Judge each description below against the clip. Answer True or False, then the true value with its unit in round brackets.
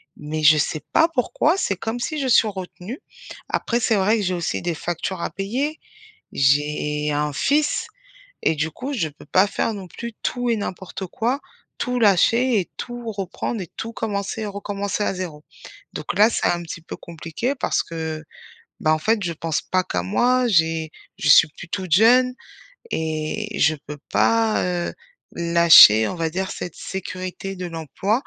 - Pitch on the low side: False (185 Hz)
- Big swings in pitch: True (5.9 semitones)